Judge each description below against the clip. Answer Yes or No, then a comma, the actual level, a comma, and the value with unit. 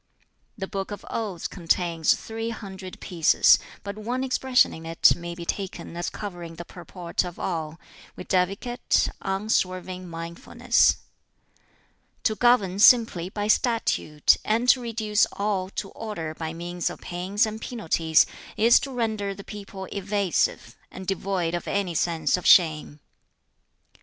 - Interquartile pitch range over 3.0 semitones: Yes, average, 3.8 semitones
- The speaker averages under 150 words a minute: Yes, slow, 135 wpm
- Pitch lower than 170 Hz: No, high, 190 Hz